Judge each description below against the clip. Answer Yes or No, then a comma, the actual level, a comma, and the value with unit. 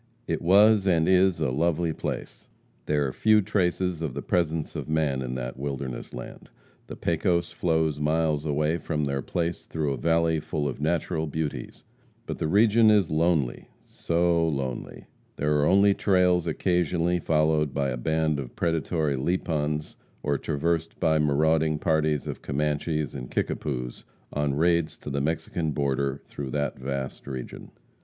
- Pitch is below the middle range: Yes, very low, 80 Hz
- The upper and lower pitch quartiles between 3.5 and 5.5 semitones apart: No, average, 2.9 semitones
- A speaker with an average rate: Yes, average, 155 wpm